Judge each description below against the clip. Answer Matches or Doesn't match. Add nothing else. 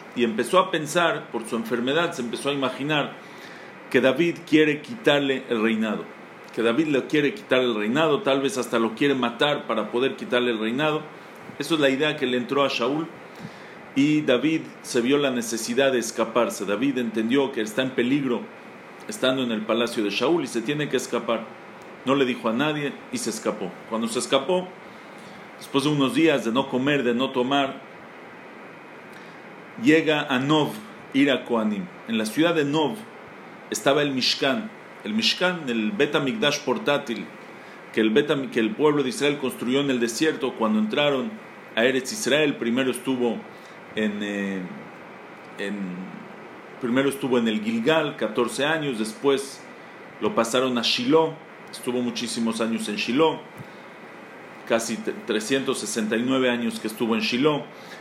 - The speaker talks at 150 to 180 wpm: Matches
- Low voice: Matches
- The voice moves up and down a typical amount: Matches